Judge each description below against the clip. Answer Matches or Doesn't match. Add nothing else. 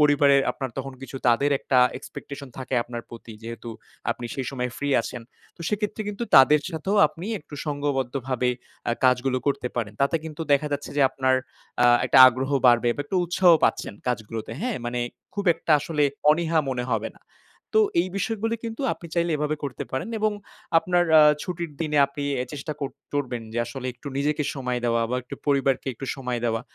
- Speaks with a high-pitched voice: Doesn't match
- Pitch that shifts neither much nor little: Matches